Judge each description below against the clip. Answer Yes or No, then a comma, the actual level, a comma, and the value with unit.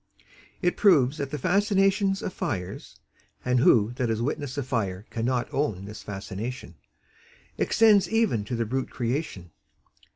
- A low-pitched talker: Yes, low, 125 Hz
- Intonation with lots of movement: Yes, wide, 8.2 semitones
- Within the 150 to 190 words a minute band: No, average, 140 wpm